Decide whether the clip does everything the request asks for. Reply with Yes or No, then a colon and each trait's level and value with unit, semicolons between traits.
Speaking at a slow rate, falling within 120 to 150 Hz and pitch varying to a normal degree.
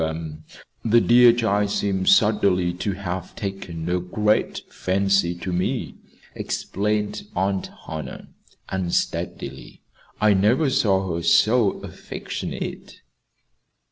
No: slow, 105 wpm; very low, 95 Hz; average, 3.1 semitones